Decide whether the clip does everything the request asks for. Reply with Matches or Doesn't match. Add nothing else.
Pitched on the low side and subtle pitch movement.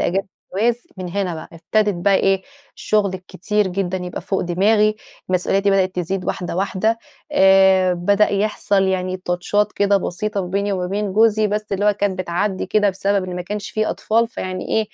Doesn't match